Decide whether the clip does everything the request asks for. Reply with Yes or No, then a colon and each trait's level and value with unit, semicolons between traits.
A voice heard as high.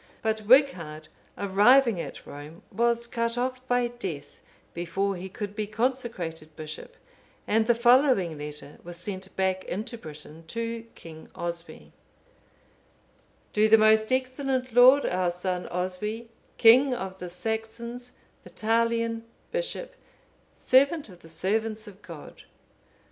Yes: high, 215 Hz